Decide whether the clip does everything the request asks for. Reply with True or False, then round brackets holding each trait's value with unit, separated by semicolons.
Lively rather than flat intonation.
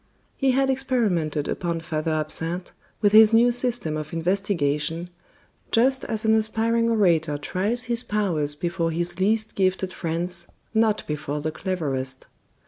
True (5.8 semitones)